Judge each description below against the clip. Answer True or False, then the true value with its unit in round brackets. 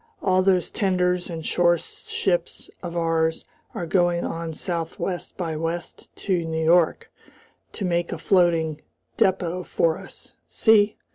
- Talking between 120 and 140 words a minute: True (135 wpm)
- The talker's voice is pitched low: False (175 Hz)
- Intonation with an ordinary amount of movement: False (1.8 semitones)